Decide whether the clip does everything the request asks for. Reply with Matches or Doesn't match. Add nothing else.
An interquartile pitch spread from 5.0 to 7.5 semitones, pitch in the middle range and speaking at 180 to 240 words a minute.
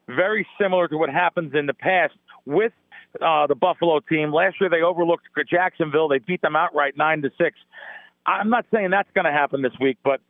Doesn't match